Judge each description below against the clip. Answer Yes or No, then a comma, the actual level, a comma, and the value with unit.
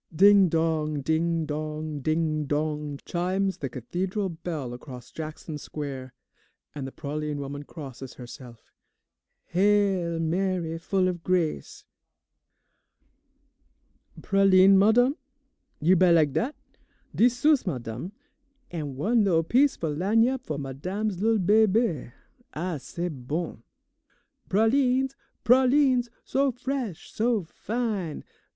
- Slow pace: Yes, slow, 110 wpm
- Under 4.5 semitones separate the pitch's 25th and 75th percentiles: No, wide, 5.6 semitones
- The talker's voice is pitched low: No, medium, 170 Hz